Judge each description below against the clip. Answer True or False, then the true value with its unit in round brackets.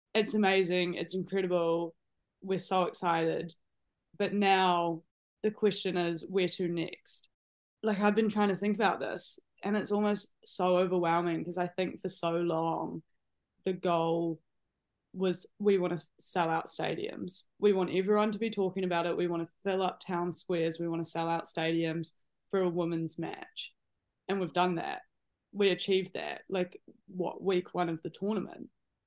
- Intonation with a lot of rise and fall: False (2.5 semitones)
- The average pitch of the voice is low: False (180 Hz)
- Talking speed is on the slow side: False (170 wpm)